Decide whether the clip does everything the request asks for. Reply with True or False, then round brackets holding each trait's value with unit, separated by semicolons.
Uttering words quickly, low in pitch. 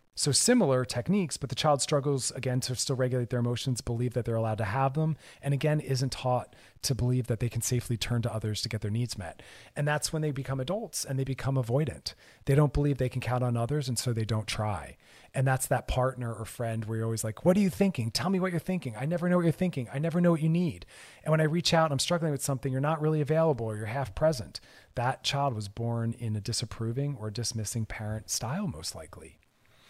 True (245 wpm; 130 Hz)